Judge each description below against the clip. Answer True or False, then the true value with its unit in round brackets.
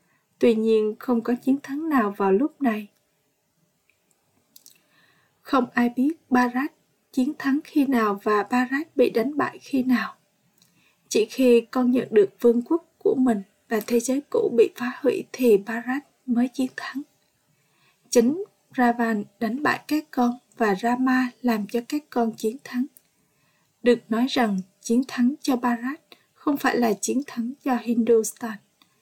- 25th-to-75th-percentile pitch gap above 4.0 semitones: False (2.7 semitones)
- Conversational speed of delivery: False (155 wpm)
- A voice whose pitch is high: True (245 Hz)